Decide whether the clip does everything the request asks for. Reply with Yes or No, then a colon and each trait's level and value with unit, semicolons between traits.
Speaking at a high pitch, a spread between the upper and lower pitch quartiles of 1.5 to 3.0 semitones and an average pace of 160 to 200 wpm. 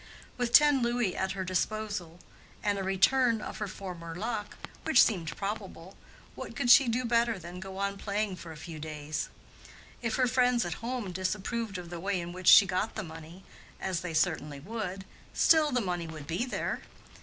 No: high, 195 Hz; average, 4.8 semitones; average, 190 wpm